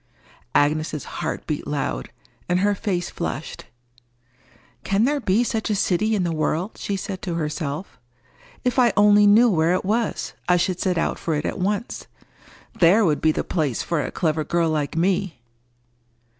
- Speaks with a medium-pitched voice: Yes, medium, 180 Hz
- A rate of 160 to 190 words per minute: Yes, average, 170 wpm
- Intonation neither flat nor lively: Yes, average, 4.6 semitones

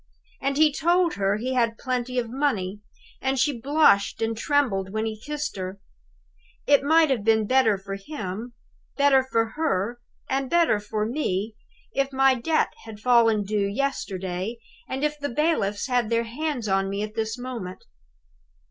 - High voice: Yes, high, 235 Hz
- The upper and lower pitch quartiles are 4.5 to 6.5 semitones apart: Yes, average, 4.8 semitones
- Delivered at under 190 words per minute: Yes, average, 165 wpm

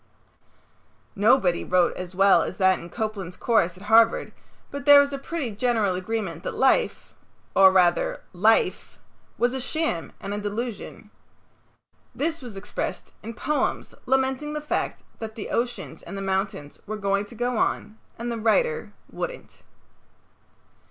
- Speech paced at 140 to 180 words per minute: Yes, average, 150 wpm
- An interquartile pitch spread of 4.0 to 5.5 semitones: Yes, average, 4.8 semitones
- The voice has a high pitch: Yes, high, 220 Hz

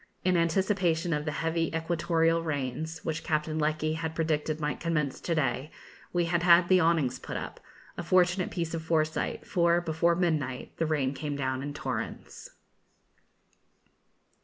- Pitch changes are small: Yes, narrow, 2.0 semitones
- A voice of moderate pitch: Yes, medium, 160 Hz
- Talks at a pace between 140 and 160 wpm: Yes, average, 155 wpm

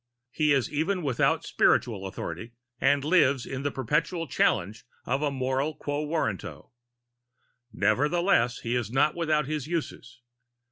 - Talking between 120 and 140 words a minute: Yes, slow, 135 wpm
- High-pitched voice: No, medium, 140 Hz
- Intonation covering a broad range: No, average, 4.1 semitones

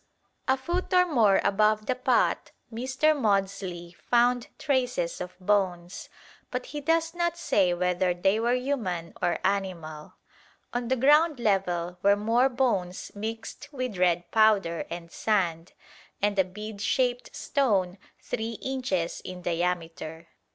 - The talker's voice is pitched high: Yes, high, 205 Hz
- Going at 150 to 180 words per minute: No, slow, 135 wpm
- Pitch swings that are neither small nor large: No, wide, 5.9 semitones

